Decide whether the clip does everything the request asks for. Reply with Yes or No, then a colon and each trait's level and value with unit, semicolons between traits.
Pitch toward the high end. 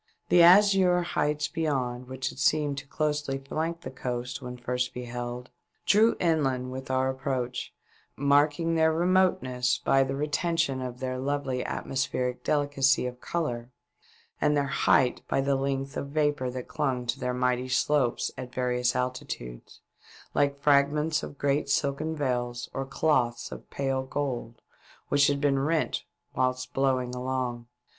No: low, 135 Hz